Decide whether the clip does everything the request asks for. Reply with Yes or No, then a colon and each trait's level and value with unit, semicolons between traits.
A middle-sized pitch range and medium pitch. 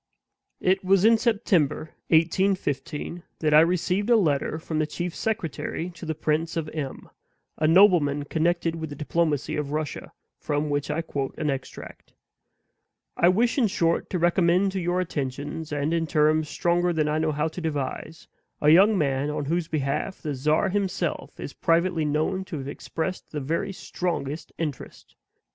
Yes: average, 3.2 semitones; medium, 160 Hz